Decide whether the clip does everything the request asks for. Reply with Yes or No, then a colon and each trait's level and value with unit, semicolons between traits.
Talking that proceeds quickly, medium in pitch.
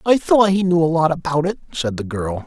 Yes: fast, 270 wpm; medium, 165 Hz